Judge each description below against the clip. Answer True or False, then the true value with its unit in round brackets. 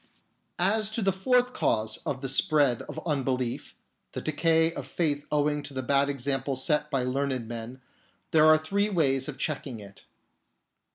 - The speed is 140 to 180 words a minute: True (175 wpm)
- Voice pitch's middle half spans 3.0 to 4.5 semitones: True (3.7 semitones)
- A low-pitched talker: False (145 Hz)